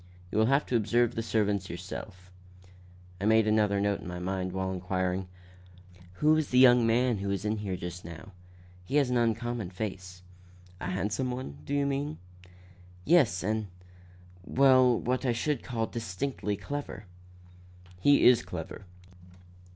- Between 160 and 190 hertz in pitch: No, low, 110 Hz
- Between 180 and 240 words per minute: No, average, 150 wpm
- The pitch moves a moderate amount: Yes, average, 4.9 semitones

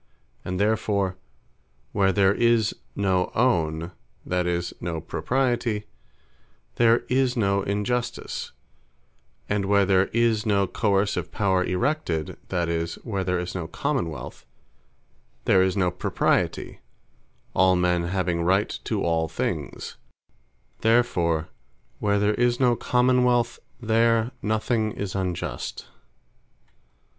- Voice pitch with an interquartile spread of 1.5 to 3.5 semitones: No, average, 4.3 semitones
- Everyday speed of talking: No, slow, 115 wpm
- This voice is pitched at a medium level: No, low, 100 Hz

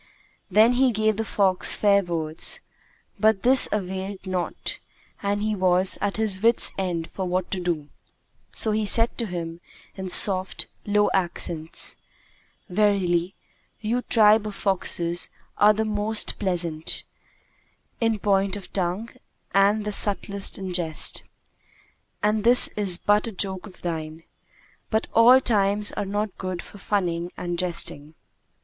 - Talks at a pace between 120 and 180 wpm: Yes, average, 145 wpm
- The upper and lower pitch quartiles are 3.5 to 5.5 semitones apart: No, average, 2.9 semitones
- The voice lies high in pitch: Yes, high, 195 Hz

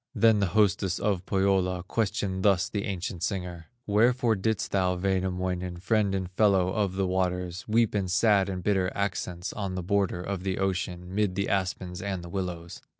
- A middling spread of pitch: No, narrow, 1.8 semitones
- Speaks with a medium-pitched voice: No, very low, 95 Hz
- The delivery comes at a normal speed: Yes, average, 175 wpm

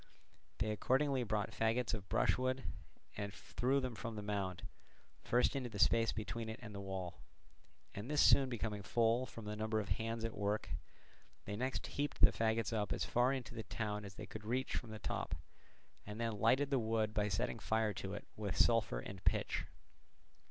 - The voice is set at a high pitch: No, low, 110 Hz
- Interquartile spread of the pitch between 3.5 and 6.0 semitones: No, narrow, 2.6 semitones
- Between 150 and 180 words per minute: No, average, 190 wpm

